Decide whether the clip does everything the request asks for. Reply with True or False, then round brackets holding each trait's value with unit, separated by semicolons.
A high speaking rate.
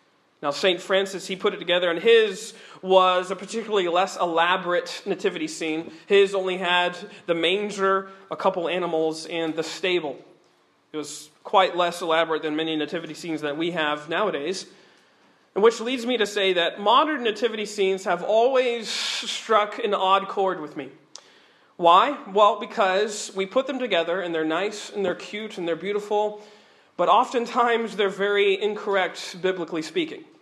False (160 wpm)